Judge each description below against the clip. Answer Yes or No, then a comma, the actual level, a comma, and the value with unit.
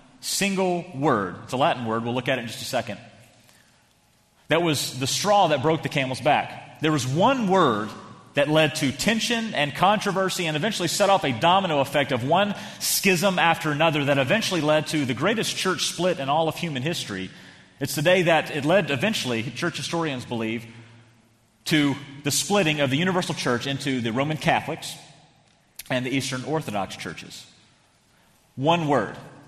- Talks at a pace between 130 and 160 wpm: No, average, 175 wpm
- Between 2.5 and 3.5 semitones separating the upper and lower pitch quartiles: No, average, 5.0 semitones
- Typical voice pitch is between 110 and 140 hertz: No, medium, 150 Hz